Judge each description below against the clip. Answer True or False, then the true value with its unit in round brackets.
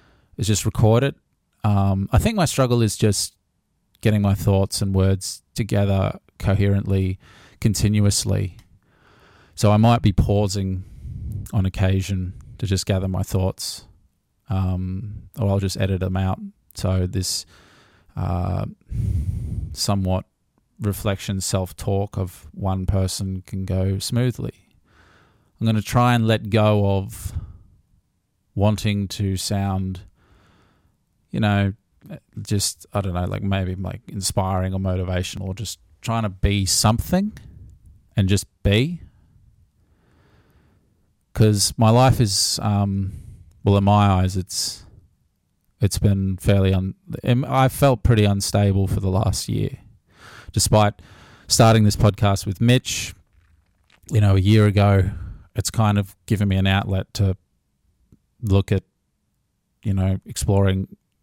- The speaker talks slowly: True (125 wpm)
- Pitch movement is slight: True (2.1 semitones)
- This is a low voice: True (100 Hz)